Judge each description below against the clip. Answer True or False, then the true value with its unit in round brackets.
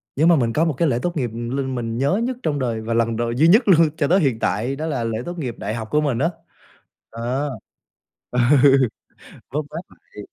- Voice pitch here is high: False (135 Hz)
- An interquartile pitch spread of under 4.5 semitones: False (5.1 semitones)